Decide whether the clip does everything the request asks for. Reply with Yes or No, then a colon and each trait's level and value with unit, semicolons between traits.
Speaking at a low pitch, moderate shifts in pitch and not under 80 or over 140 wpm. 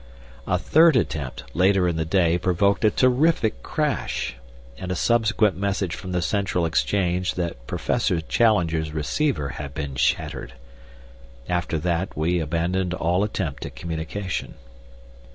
Yes: very low, 90 Hz; average, 3.8 semitones; slow, 135 wpm